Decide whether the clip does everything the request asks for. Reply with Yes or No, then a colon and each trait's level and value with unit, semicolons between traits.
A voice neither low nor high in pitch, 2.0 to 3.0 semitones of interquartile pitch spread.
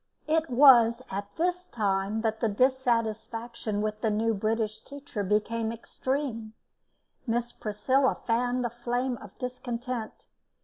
No: high, 230 Hz; average, 2.7 semitones